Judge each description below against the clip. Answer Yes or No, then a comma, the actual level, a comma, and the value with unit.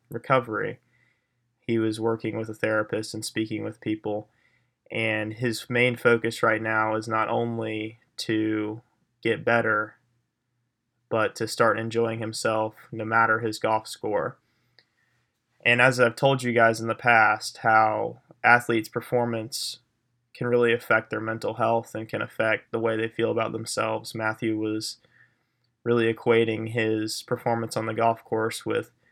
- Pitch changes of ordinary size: No, narrow, 1.5 semitones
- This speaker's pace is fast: No, average, 145 wpm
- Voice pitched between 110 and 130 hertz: Yes, low, 115 Hz